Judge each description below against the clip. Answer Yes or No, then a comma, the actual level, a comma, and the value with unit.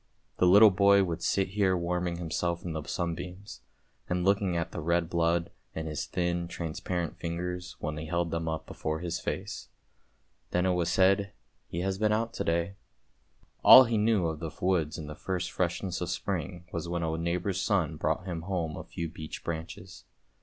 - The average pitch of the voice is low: Yes, very low, 85 Hz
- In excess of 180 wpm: Yes, average, 190 wpm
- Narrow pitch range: Yes, narrow, 2.1 semitones